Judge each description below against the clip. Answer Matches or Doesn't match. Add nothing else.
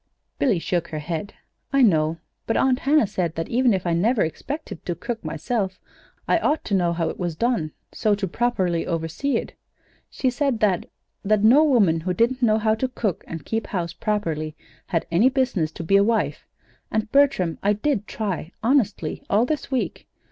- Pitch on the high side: Matches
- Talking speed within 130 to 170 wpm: Doesn't match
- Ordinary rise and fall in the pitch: Doesn't match